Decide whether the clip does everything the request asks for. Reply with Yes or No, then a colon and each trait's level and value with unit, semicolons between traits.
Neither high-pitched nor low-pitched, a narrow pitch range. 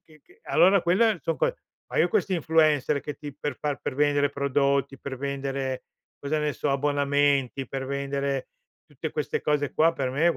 Yes: medium, 145 Hz; narrow, 2.0 semitones